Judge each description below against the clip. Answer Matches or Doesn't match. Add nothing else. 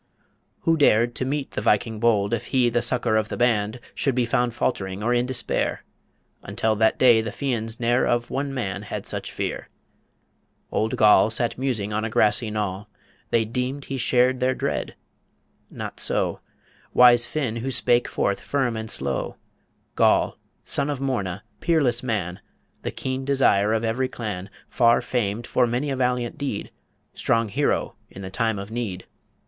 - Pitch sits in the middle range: Doesn't match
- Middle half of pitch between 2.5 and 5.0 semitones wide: Matches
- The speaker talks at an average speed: Matches